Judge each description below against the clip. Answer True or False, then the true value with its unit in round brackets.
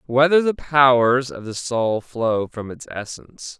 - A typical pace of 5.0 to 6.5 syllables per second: False (4.1 syllables/s)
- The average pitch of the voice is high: False (125 Hz)